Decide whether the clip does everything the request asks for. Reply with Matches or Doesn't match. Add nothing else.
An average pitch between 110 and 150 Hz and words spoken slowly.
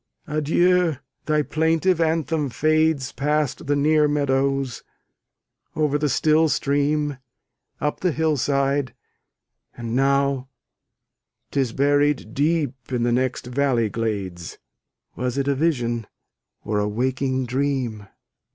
Matches